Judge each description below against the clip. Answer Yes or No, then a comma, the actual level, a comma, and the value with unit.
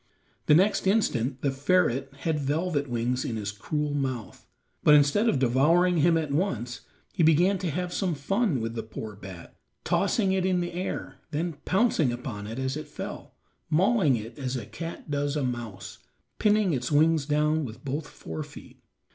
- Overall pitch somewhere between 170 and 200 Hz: No, medium, 145 Hz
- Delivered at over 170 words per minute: Yes, average, 180 wpm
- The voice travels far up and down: Yes, wide, 5.9 semitones